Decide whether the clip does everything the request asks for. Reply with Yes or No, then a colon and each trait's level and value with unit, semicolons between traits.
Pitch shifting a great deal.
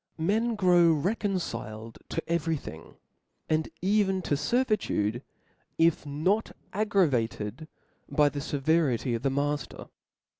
Yes: wide, 5.9 semitones